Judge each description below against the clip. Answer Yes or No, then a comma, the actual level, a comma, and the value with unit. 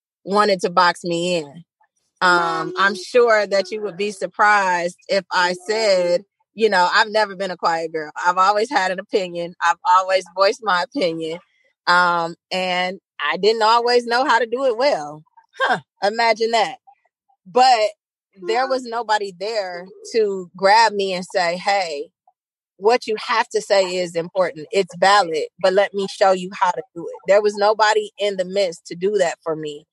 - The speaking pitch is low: No, high, 195 Hz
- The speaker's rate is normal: Yes, average, 175 wpm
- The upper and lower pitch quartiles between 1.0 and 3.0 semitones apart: No, average, 3.6 semitones